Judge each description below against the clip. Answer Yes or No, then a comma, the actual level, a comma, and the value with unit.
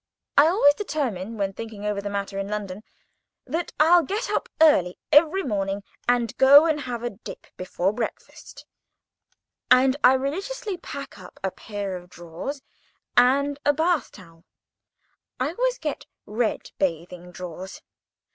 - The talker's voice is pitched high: Yes, high, 240 Hz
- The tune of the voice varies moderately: No, wide, 7.1 semitones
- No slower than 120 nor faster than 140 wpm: Yes, slow, 135 wpm